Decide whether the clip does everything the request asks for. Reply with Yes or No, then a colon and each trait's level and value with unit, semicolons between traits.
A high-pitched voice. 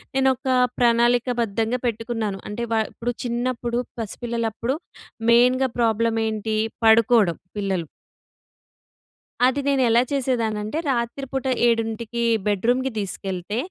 Yes: high, 235 Hz